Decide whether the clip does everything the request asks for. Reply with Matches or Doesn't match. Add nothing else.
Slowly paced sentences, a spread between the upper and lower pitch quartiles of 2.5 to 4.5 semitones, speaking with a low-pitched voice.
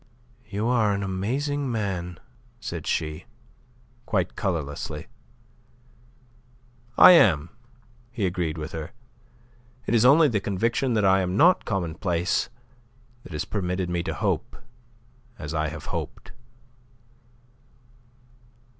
Doesn't match